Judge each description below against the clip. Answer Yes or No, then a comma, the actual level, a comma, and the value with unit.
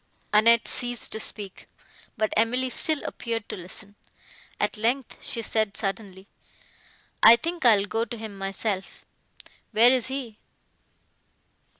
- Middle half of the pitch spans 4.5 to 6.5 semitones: No, average, 2.8 semitones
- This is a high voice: Yes, high, 225 Hz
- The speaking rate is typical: No, slow, 125 wpm